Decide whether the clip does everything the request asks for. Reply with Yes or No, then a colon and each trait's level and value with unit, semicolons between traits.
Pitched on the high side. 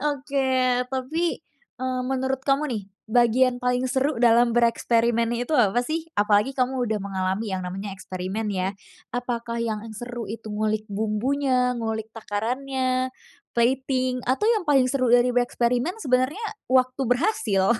Yes: high, 245 Hz